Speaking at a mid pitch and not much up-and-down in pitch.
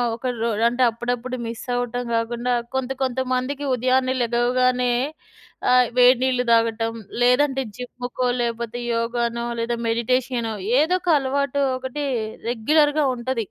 No: high, 245 Hz; narrow, 1.6 semitones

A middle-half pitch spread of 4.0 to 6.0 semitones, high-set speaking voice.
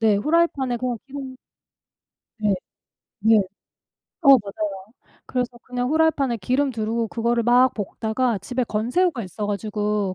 No: average, 3.5 semitones; high, 235 Hz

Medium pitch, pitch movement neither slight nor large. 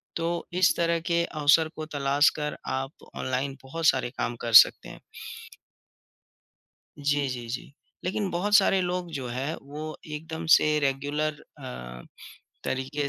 Yes: medium, 150 Hz; average, 3.7 semitones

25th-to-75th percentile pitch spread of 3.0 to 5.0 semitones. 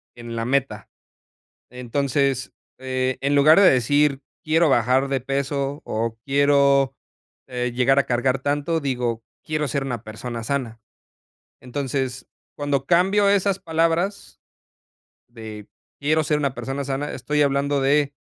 No: narrow, 2.5 semitones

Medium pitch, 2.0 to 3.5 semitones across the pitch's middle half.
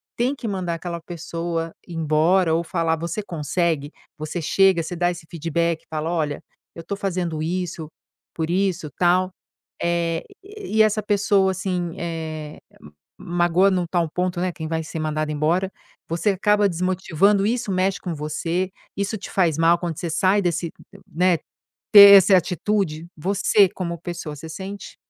Yes: medium, 175 Hz; average, 2.7 semitones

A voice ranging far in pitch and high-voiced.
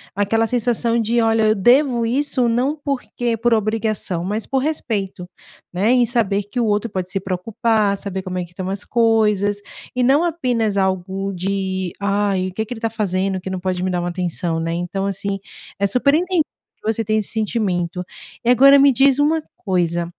No: average, 4.1 semitones; high, 210 Hz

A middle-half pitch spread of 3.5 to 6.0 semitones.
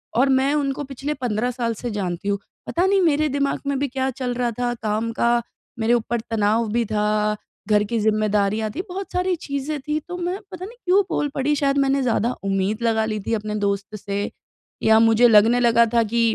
Yes: average, 4.7 semitones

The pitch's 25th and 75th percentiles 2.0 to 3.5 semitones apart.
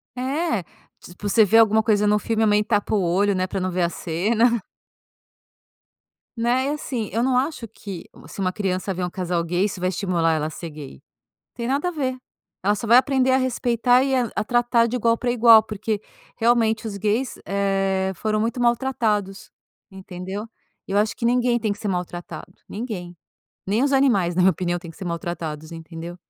No: average, 4.5 semitones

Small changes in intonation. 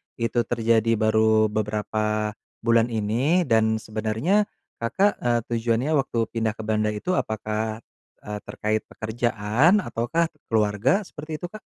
Yes: narrow, 2.0 semitones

